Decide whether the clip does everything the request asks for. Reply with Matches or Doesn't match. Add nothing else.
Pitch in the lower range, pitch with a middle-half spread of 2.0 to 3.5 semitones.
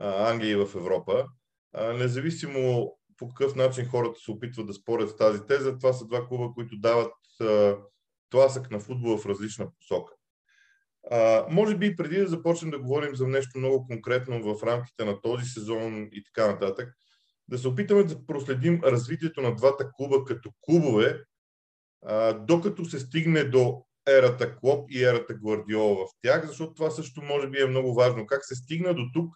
Doesn't match